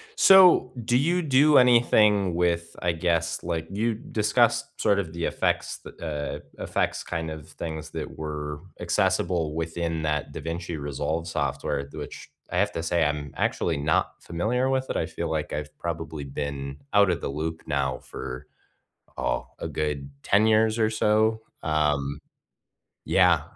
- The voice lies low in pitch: Yes, very low, 80 Hz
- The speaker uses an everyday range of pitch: No, wide, 5.8 semitones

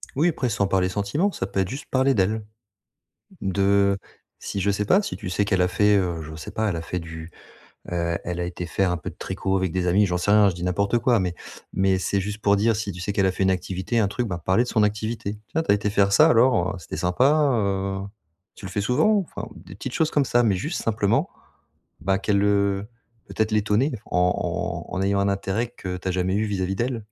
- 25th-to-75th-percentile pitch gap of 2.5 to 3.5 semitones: Yes, average, 2.8 semitones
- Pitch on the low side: Yes, low, 100 Hz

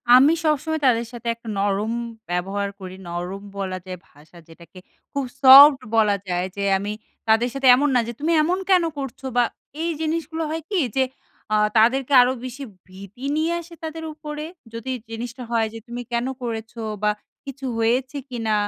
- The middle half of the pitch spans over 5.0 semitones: Yes, wide, 5.6 semitones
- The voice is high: Yes, high, 240 Hz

